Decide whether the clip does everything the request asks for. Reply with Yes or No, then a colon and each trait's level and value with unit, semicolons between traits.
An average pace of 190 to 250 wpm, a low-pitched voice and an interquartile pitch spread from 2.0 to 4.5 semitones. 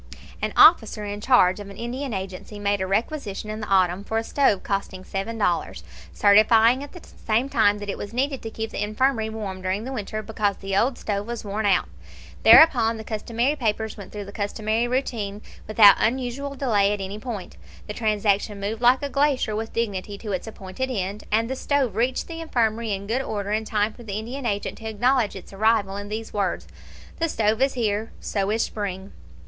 No: fast, 205 wpm; high, 215 Hz; average, 2.9 semitones